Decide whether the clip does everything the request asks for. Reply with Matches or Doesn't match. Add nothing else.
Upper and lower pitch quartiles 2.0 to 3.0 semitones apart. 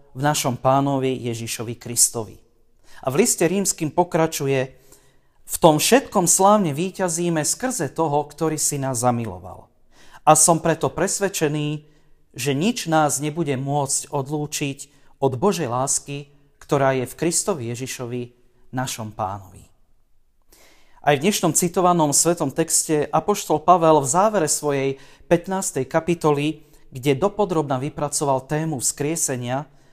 Doesn't match